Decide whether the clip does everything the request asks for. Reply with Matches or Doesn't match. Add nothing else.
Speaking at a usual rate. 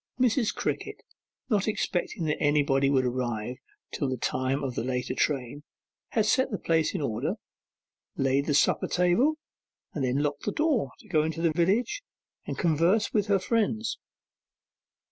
Matches